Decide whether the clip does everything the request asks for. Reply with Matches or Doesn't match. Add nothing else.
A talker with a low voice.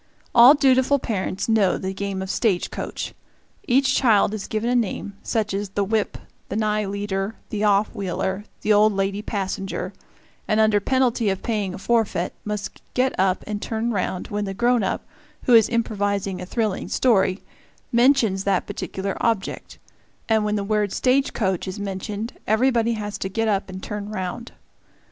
Doesn't match